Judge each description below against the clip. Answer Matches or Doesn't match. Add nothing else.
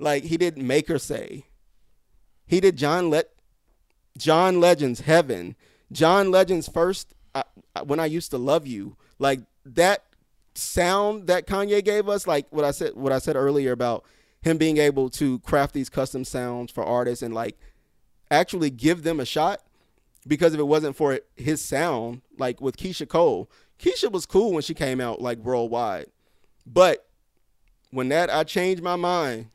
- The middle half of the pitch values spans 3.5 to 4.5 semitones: Doesn't match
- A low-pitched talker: Doesn't match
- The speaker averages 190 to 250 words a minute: Doesn't match